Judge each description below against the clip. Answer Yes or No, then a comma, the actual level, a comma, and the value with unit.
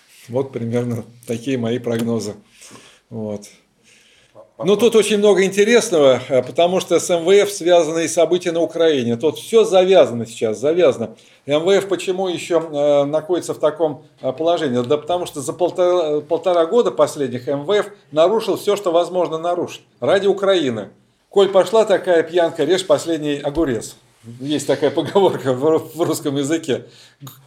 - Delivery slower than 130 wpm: No, average, 135 wpm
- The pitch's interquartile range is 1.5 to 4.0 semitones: No, average, 4.8 semitones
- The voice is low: No, medium, 160 Hz